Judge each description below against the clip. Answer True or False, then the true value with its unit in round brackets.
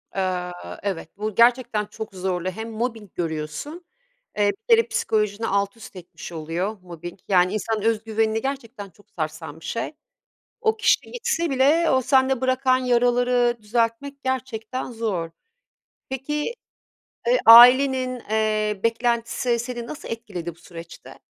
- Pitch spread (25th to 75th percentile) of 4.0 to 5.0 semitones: True (4.5 semitones)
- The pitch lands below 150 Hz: False (225 Hz)